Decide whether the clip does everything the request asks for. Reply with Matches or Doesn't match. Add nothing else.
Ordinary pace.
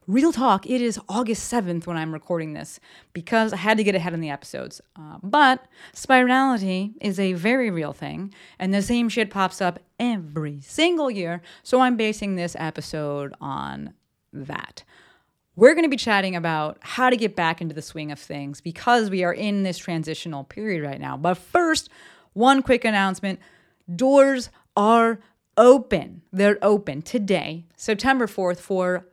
Matches